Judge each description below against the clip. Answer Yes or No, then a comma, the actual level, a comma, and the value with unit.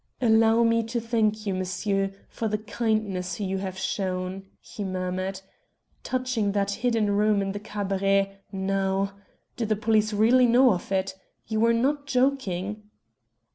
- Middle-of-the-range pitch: No, high, 205 Hz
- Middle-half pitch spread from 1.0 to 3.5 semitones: Yes, average, 2.8 semitones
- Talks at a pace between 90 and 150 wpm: Yes, average, 145 wpm